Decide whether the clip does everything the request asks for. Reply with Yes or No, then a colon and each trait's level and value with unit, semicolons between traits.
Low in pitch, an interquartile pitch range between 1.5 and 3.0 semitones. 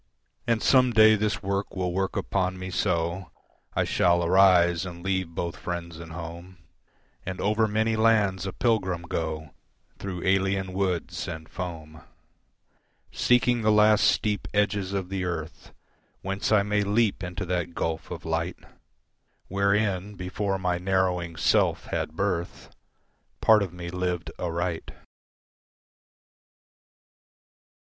Yes: very low, 95 Hz; average, 2.7 semitones